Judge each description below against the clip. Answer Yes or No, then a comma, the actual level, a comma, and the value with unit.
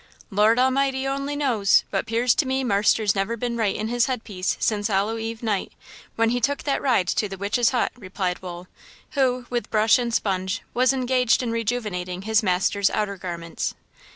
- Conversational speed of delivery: Yes, average, 180 wpm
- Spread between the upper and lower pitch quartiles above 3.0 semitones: Yes, average, 3.9 semitones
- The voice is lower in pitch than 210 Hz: No, high, 225 Hz